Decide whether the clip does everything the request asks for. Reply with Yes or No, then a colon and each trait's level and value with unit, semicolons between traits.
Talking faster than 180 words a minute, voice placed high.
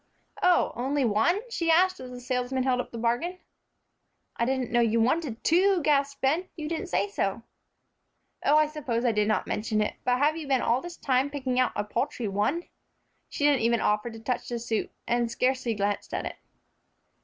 Yes: average, 200 wpm; very high, 255 Hz